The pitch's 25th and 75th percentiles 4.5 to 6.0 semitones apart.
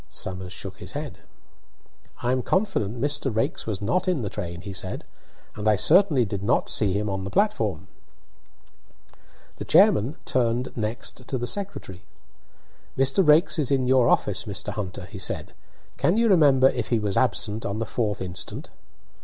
Yes: wide, 5.6 semitones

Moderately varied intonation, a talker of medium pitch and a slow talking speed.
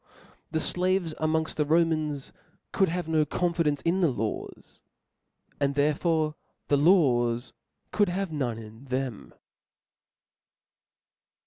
Yes: average, 3.8 semitones; medium, 155 Hz; slow, 115 wpm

